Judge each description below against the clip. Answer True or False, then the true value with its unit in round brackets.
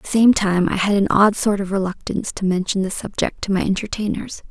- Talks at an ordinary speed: False (240 wpm)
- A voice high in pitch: True (200 Hz)